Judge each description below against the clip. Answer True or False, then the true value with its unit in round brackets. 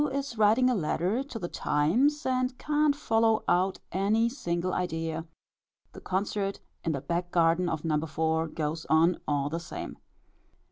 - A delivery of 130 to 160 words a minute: True (155 wpm)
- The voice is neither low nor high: True (180 Hz)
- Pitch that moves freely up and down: True (6.1 semitones)